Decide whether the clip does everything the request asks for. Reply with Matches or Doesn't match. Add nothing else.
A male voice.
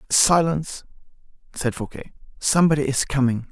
Matches